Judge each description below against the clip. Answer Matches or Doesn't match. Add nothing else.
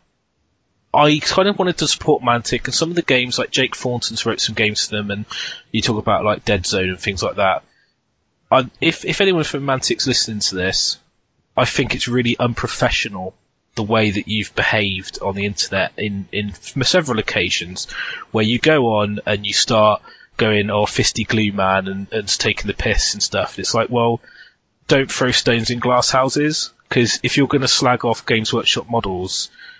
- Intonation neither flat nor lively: Matches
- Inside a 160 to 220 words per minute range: Matches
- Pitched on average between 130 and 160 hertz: Doesn't match